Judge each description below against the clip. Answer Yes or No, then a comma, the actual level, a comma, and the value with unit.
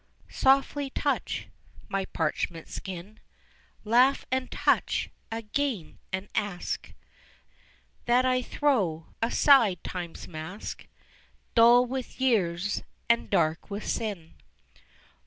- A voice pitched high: Yes, high, 215 Hz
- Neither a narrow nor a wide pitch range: No, wide, 6.1 semitones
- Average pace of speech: No, slow, 95 wpm